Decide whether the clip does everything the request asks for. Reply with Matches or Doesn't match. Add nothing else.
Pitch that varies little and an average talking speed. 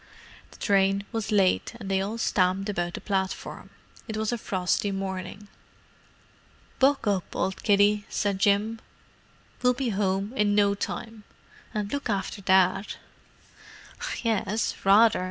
Doesn't match